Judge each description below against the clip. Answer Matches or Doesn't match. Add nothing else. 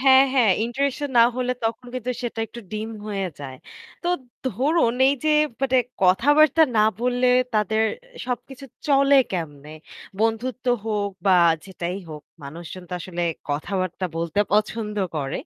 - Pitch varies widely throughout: Matches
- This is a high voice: Matches